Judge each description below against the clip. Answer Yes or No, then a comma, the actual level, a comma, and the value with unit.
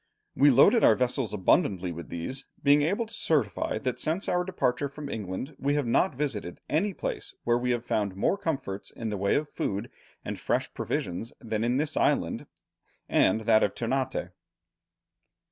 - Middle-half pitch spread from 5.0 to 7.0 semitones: Yes, wide, 5.6 semitones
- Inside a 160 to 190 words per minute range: Yes, average, 175 wpm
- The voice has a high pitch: No, low, 125 Hz